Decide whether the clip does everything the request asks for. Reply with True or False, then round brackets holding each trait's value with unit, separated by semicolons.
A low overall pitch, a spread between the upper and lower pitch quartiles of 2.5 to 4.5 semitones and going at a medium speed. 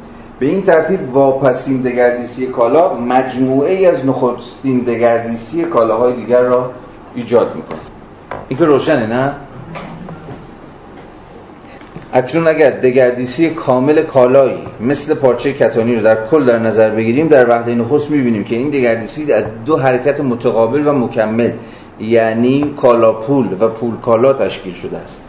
True (125 Hz; 3.3 semitones; 135 wpm)